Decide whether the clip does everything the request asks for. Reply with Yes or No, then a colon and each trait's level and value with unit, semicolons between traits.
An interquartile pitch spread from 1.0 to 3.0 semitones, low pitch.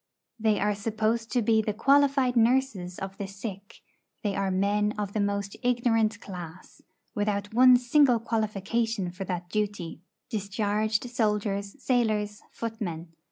No: narrow, 2.6 semitones; high, 210 Hz